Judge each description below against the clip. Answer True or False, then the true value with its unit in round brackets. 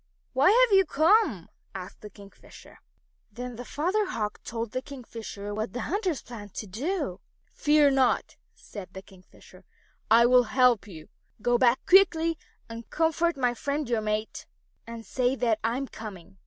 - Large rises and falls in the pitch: True (5.7 semitones)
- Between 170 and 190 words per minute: False (160 wpm)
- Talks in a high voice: True (245 Hz)